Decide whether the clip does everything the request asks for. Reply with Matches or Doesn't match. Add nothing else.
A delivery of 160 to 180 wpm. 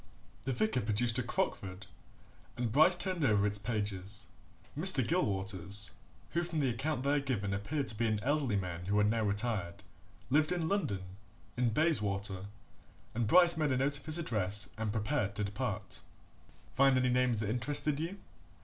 Matches